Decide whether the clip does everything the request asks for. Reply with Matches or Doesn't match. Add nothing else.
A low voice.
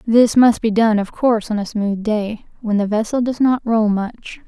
Doesn't match